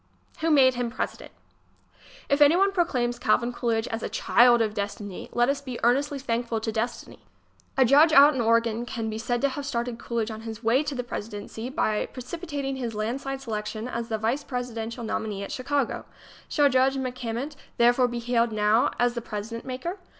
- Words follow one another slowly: No, average, 185 wpm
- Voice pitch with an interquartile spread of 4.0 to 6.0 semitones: No, average, 3.0 semitones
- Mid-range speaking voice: No, high, 240 Hz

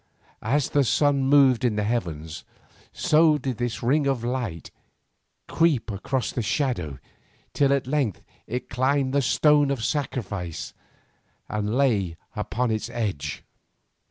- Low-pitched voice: Yes, low, 125 Hz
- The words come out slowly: Yes, slow, 130 wpm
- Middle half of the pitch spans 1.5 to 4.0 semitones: No, average, 4.7 semitones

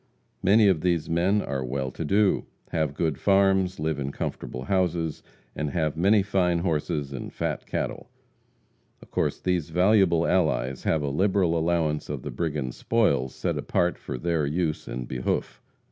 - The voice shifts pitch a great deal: No, average, 4.4 semitones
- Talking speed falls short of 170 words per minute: Yes, average, 160 wpm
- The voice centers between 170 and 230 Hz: No, very low, 80 Hz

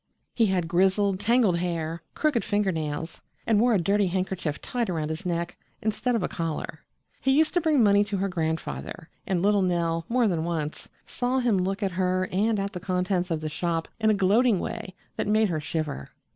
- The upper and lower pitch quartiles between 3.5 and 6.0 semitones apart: Yes, average, 4.1 semitones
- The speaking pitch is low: No, medium, 185 Hz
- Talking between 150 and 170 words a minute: No, average, 200 wpm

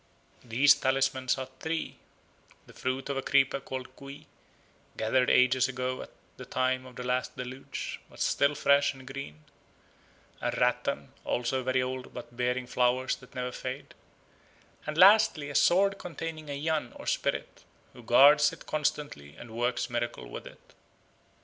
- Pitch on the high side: No, low, 130 Hz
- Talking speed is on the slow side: No, average, 155 wpm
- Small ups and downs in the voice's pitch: Yes, narrow, 2.2 semitones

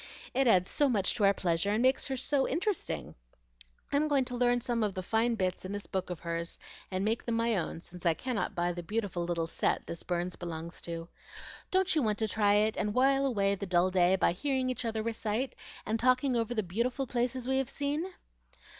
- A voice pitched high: Yes, high, 220 Hz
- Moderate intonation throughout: No, wide, 5.7 semitones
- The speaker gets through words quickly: Yes, fast, 220 wpm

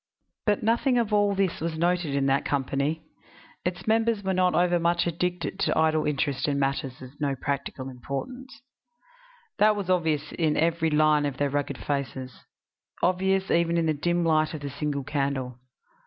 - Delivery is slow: No, average, 170 wpm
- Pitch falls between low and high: Yes, medium, 160 Hz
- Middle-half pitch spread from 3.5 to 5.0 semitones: Yes, average, 4.2 semitones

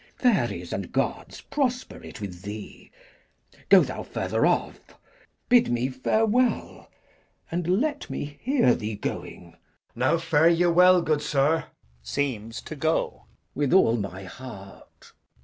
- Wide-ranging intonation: Yes, wide, 8.4 semitones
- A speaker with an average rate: No, slow, 125 wpm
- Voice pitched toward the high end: No, medium, 145 Hz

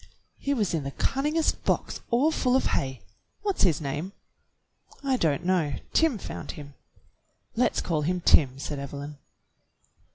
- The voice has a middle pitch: Yes, medium, 175 Hz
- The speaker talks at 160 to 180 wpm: No, average, 150 wpm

